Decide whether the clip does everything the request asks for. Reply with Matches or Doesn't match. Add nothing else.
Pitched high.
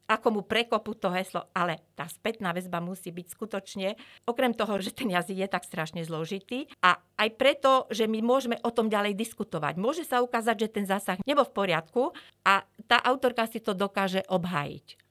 Matches